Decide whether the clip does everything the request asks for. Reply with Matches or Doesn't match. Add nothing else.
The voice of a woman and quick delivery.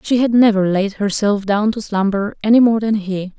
Matches